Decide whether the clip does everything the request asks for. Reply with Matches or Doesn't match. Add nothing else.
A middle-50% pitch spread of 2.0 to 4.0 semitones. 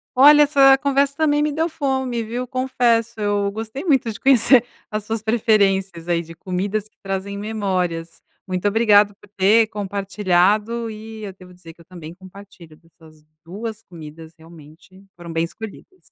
Doesn't match